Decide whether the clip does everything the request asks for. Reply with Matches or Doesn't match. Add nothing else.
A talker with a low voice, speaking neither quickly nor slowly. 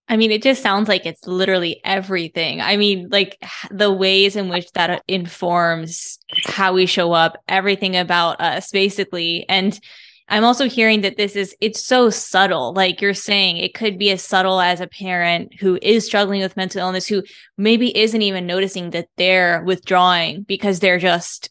Doesn't match